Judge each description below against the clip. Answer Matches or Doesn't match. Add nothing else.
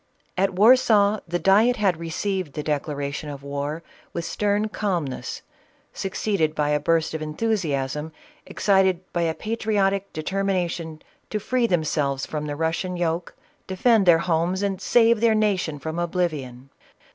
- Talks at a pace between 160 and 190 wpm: Doesn't match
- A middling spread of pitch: Matches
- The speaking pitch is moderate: Matches